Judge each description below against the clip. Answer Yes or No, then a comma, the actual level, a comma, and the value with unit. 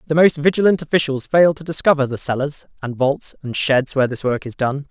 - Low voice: No, medium, 145 Hz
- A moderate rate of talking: No, fast, 220 wpm